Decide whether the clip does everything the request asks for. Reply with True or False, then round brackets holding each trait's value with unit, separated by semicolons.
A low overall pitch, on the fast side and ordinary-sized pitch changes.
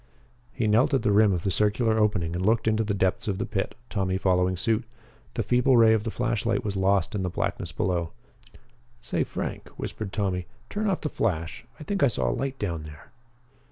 True (105 Hz; 210 wpm; 3.7 semitones)